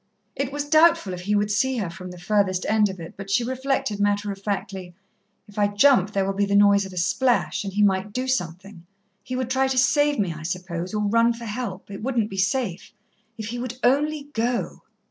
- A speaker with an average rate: No, fast, 225 wpm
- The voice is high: Yes, high, 205 Hz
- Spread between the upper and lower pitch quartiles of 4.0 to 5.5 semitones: Yes, average, 4.7 semitones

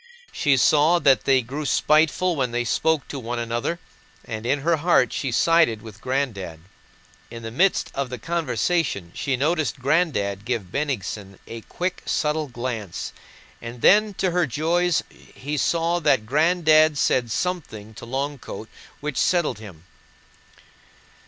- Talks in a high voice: No, medium, 140 Hz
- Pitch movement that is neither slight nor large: No, wide, 5.7 semitones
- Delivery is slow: No, average, 145 wpm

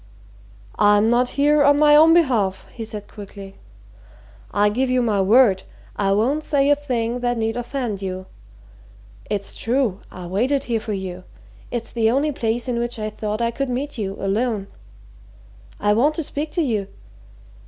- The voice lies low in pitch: No, high, 235 Hz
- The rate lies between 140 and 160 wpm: No, average, 170 wpm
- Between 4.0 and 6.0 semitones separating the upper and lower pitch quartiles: Yes, average, 4.4 semitones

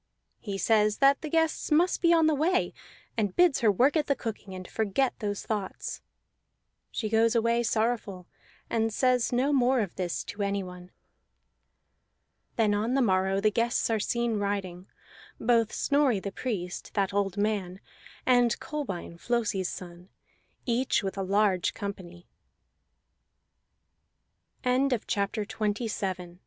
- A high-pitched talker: Yes, high, 215 Hz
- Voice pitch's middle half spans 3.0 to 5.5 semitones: Yes, average, 4.0 semitones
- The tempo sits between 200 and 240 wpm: No, slow, 135 wpm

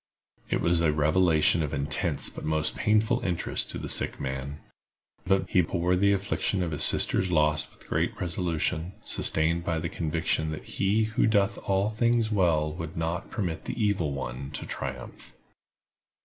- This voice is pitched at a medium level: No, very low, 85 Hz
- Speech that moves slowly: No, average, 165 wpm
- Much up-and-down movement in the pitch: No, average, 3.9 semitones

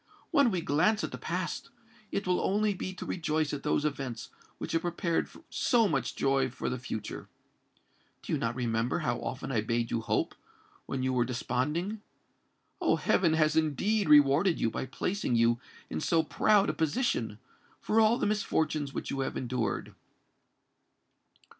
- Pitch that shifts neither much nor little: No, wide, 6.4 semitones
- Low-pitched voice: No, medium, 150 Hz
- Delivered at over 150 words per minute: Yes, average, 165 wpm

